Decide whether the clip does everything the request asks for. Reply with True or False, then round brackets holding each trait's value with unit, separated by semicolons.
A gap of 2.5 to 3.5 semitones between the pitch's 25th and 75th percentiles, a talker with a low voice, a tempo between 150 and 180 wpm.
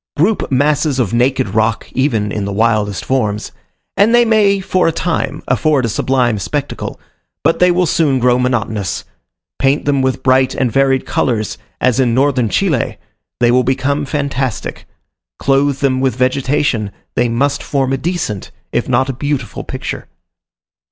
True (3.2 semitones; 130 Hz; 160 wpm)